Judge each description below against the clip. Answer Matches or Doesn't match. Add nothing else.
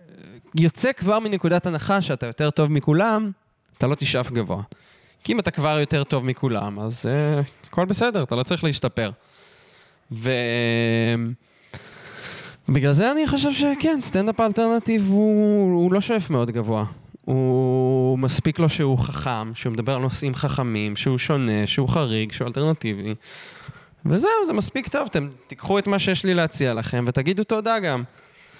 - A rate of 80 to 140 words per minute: Doesn't match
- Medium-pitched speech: Matches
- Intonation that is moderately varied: Doesn't match